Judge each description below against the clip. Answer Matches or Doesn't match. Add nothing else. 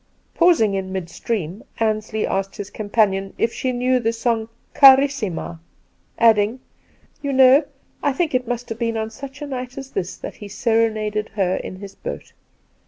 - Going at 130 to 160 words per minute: Doesn't match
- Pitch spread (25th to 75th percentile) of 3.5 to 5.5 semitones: Matches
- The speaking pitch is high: Matches